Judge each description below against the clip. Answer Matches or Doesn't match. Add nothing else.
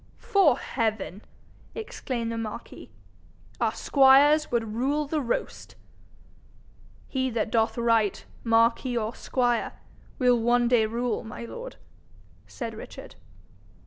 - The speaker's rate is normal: Doesn't match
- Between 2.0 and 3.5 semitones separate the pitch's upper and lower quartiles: Matches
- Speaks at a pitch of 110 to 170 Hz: Doesn't match